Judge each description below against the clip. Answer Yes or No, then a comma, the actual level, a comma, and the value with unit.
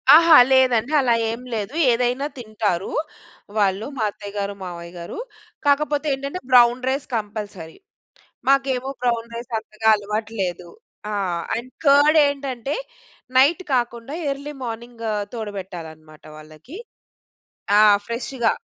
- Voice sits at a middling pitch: No, high, 235 Hz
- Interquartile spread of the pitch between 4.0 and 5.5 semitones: Yes, average, 4.8 semitones